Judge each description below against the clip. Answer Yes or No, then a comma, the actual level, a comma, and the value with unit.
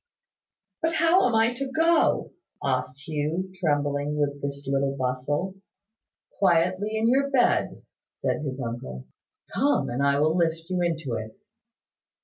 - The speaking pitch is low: No, medium, 160 Hz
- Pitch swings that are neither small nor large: No, wide, 7.3 semitones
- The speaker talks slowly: Yes, slow, 130 wpm